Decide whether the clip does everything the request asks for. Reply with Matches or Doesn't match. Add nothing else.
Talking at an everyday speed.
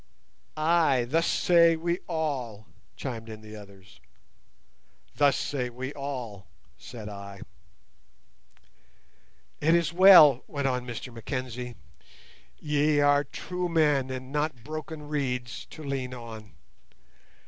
Doesn't match